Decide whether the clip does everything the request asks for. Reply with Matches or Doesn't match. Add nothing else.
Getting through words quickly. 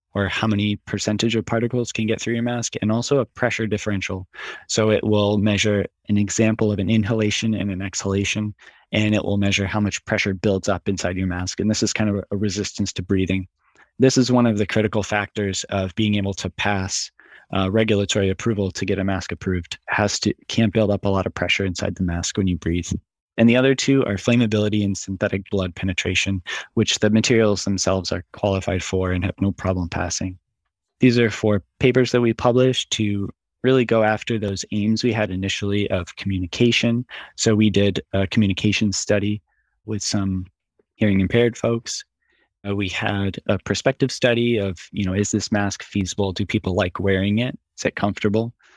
Doesn't match